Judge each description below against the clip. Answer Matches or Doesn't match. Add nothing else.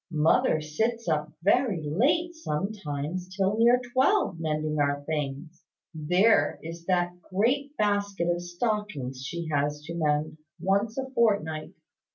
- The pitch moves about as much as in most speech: Doesn't match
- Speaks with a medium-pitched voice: Matches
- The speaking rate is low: Matches